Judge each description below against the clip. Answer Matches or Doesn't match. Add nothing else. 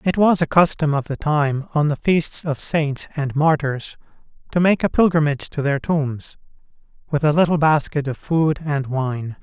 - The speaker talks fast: Doesn't match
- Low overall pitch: Doesn't match